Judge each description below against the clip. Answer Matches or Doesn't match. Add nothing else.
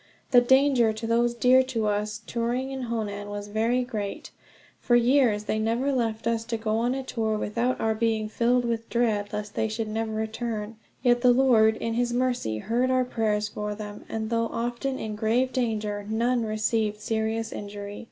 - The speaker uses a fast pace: Doesn't match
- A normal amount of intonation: Doesn't match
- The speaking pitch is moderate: Doesn't match